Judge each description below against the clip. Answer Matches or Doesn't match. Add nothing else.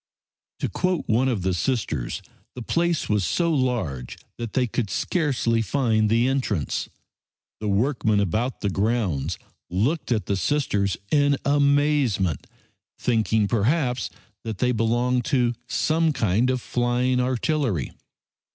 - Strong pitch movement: Doesn't match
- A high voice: Doesn't match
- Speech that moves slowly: Matches